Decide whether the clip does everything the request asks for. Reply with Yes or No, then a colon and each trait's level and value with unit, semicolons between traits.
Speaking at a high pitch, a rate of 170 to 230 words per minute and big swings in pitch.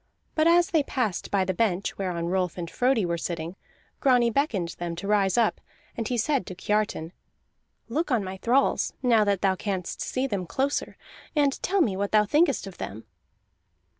Yes: high, 210 Hz; average, 185 wpm; wide, 5.9 semitones